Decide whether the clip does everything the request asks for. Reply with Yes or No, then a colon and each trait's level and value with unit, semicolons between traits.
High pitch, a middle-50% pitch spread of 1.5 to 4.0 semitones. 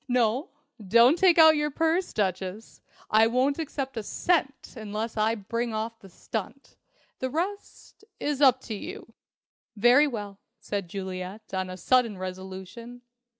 No: high, 230 Hz; wide, 5.5 semitones